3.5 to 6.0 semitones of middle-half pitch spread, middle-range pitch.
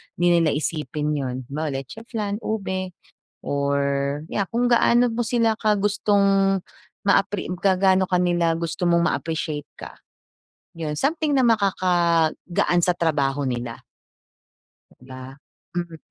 Yes: average, 5.0 semitones; medium, 175 Hz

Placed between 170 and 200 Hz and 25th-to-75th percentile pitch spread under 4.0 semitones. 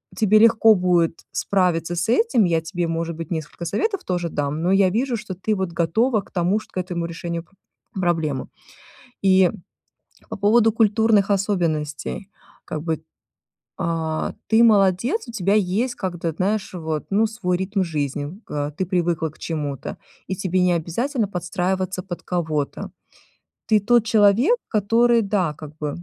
No: medium, 185 Hz; average, 4.3 semitones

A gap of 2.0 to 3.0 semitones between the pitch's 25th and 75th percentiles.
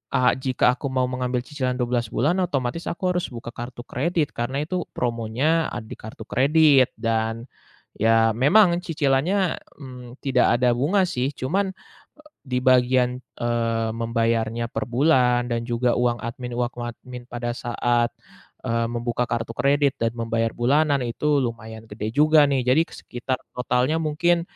No: average, 3.4 semitones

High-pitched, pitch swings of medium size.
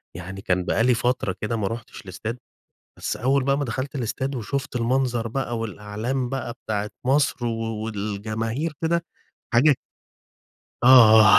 No: low, 115 Hz; average, 3.5 semitones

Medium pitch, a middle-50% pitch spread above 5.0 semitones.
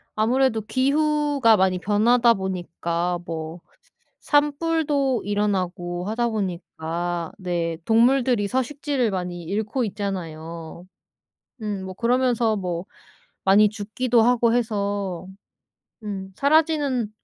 No: high, 210 Hz; wide, 5.6 semitones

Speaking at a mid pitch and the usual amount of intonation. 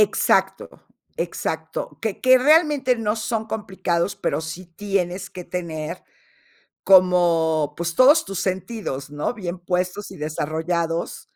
Yes: medium, 180 Hz; average, 4.1 semitones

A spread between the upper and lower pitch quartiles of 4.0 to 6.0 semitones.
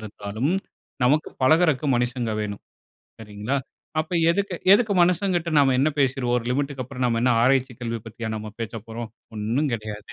Yes: average, 4.5 semitones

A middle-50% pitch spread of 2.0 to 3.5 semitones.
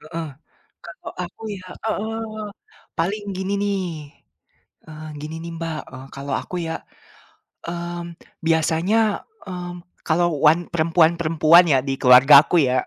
Yes: average, 2.9 semitones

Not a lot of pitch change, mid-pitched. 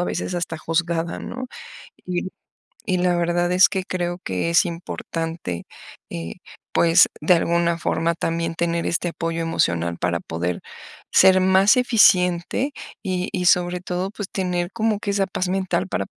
Yes: narrow, 1.9 semitones; medium, 175 Hz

